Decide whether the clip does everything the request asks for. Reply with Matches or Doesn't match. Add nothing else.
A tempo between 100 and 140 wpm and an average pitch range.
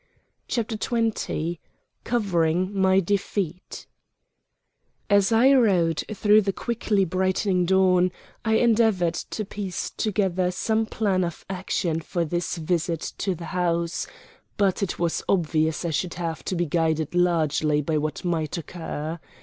Matches